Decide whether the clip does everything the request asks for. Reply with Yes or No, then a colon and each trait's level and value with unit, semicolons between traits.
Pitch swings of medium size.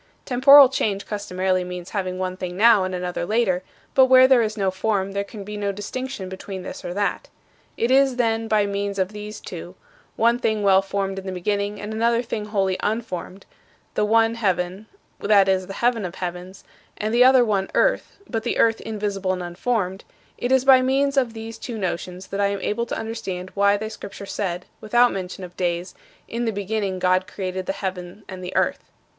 Yes: average, 3.2 semitones